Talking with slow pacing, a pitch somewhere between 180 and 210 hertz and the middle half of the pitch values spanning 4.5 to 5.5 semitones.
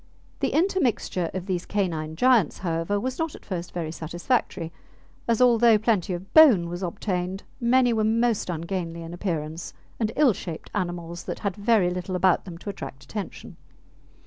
No: average, 165 wpm; medium, 185 Hz; average, 4.9 semitones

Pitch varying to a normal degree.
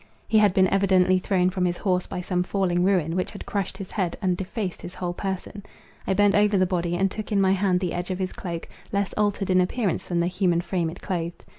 No: narrow, 1.8 semitones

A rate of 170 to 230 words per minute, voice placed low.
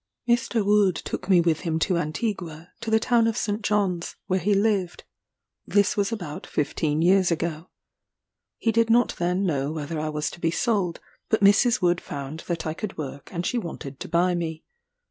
No: average, 190 wpm; medium, 180 Hz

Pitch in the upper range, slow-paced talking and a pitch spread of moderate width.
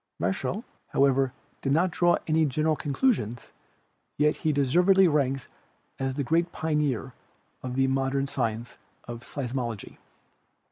No: low, 135 Hz; slow, 130 wpm; average, 3.5 semitones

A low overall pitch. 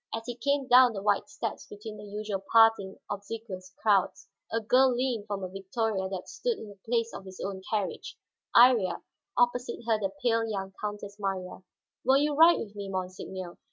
No: high, 210 Hz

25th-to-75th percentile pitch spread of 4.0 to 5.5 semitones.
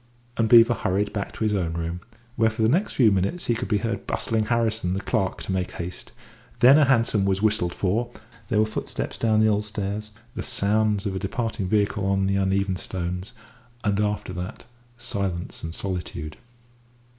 No: average, 2.8 semitones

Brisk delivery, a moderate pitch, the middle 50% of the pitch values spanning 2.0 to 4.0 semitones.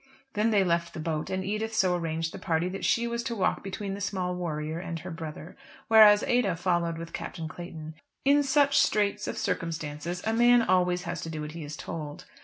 No: fast, 210 wpm; medium, 180 Hz; average, 4.4 semitones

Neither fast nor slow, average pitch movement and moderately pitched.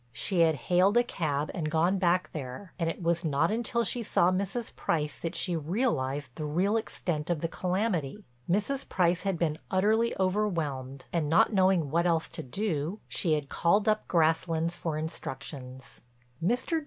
Yes: average, 170 wpm; average, 4.3 semitones; medium, 170 Hz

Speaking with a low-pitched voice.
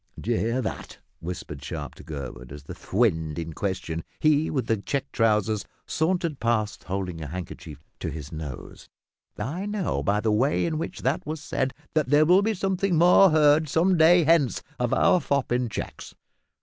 Yes: low, 125 Hz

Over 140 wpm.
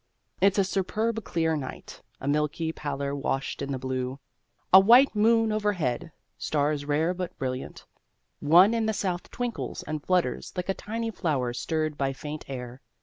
Yes: average, 160 wpm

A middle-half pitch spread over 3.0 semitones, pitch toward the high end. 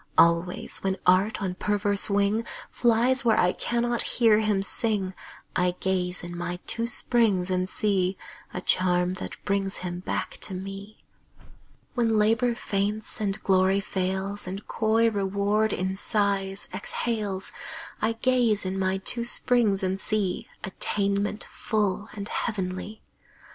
No: narrow, 2.6 semitones; high, 200 Hz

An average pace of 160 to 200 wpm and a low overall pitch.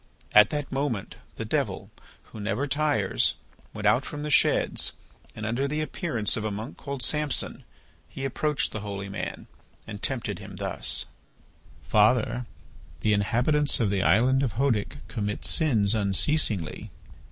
No: average, 145 wpm; low, 115 Hz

